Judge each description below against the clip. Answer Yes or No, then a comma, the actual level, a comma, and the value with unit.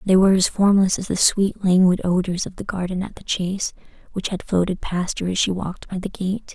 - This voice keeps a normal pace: No, fast, 240 wpm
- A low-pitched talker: No, medium, 185 Hz